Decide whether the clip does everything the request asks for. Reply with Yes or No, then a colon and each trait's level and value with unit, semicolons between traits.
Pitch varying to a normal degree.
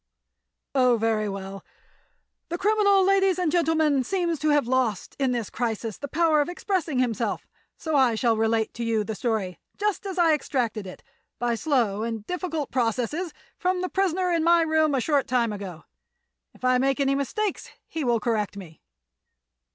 No: wide, 6.7 semitones